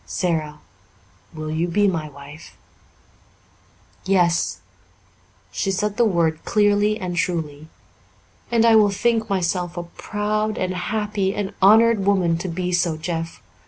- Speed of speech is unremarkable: No, slow, 130 wpm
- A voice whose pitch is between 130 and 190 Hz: Yes, medium, 185 Hz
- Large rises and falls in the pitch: No, average, 3.8 semitones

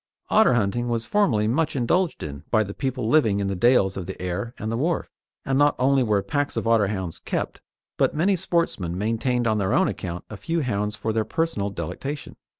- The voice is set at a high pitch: No, low, 115 Hz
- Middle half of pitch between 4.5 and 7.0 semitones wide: Yes, wide, 5.6 semitones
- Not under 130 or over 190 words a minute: No, fast, 205 wpm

